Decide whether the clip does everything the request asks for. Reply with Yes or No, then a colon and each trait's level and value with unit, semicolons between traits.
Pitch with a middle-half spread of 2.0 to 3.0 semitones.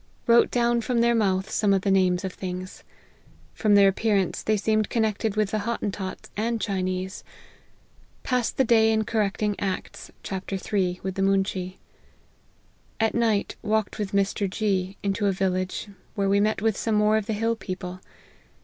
Yes: narrow, 2.4 semitones